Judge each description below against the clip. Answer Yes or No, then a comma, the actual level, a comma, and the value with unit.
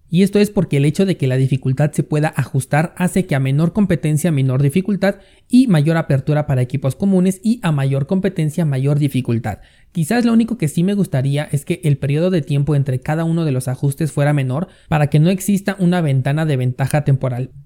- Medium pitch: Yes, medium, 150 Hz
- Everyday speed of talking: No, fast, 210 wpm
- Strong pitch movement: No, average, 4.6 semitones